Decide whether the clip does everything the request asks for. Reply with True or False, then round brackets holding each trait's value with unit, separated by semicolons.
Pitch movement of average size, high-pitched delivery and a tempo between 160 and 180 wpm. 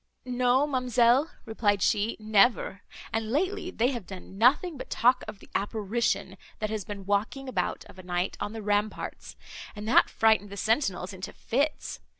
True (3.8 semitones; 220 Hz; 165 wpm)